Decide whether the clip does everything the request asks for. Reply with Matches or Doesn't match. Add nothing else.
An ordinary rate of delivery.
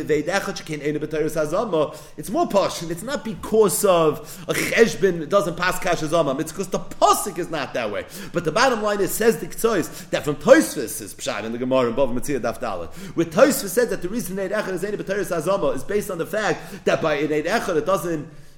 Matches